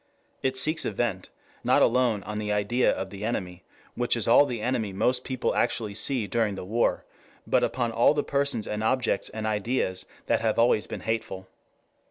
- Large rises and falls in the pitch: No, average, 3.4 semitones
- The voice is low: Yes, low, 110 Hz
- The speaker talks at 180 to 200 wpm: Yes, average, 190 wpm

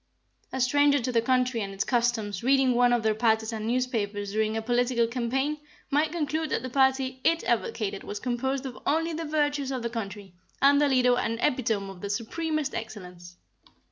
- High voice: Yes, high, 245 Hz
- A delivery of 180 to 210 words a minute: Yes, average, 185 wpm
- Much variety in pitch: No, average, 3.9 semitones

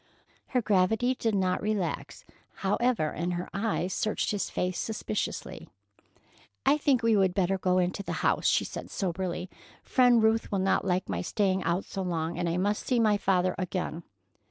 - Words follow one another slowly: No, average, 175 wpm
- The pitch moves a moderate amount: Yes, average, 3.4 semitones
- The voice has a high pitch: Yes, high, 195 Hz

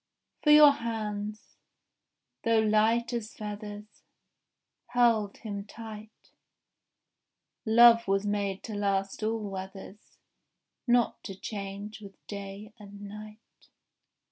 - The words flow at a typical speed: No, slow, 100 wpm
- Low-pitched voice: No, high, 210 Hz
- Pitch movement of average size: No, narrow, 2.1 semitones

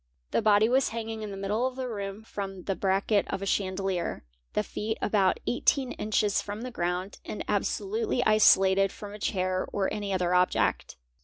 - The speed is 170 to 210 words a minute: Yes, average, 180 wpm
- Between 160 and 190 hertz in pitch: No, high, 205 Hz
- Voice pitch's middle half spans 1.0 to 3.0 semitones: Yes, narrow, 2.4 semitones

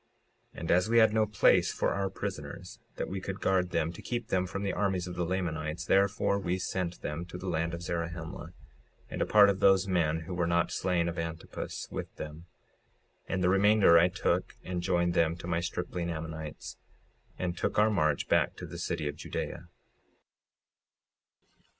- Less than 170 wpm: No, average, 190 wpm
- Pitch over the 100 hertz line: No, very low, 90 Hz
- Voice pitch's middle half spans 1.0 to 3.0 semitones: Yes, narrow, 2.4 semitones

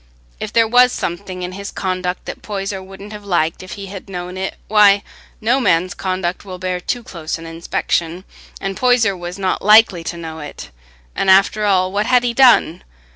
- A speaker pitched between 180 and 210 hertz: Yes, high, 190 Hz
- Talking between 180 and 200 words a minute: Yes, average, 190 wpm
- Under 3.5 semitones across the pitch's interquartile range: Yes, average, 2.7 semitones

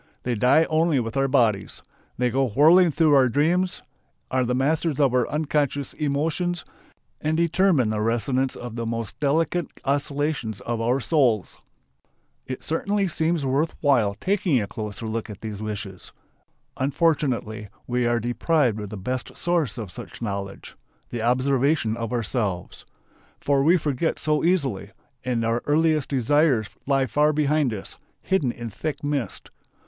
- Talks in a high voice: No, low, 135 Hz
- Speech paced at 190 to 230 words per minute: No, average, 150 wpm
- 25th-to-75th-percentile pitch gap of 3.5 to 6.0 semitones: Yes, average, 5.0 semitones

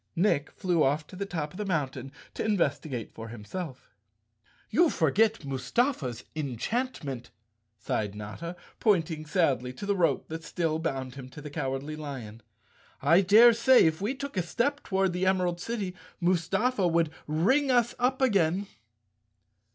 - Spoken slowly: No, average, 150 wpm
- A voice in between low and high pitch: Yes, medium, 170 Hz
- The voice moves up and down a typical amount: No, wide, 6.5 semitones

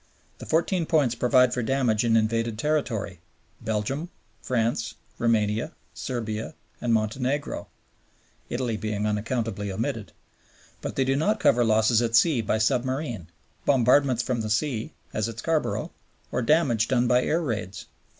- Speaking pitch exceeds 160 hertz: No, low, 120 Hz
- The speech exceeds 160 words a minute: No, average, 140 wpm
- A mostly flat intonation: No, average, 3.5 semitones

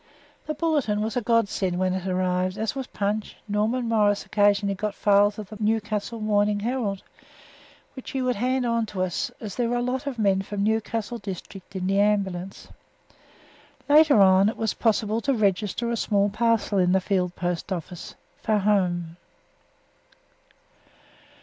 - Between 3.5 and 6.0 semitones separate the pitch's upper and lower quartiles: No, average, 3.0 semitones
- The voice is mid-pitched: No, high, 210 Hz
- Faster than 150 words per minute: Yes, average, 170 wpm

